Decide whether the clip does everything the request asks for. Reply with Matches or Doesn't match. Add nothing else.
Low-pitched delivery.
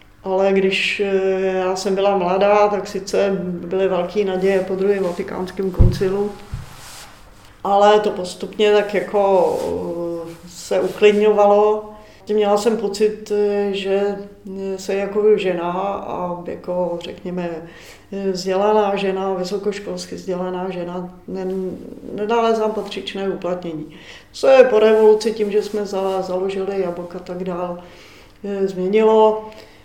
Doesn't match